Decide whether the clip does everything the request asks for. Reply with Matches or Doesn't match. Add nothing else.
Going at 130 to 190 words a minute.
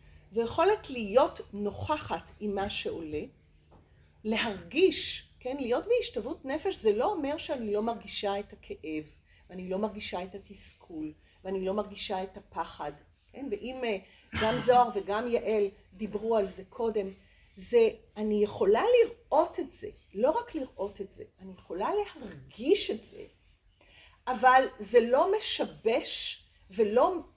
Matches